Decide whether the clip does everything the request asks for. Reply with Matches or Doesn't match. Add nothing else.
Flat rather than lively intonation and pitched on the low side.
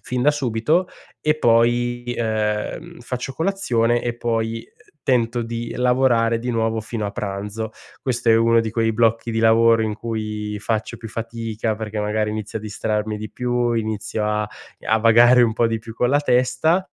Matches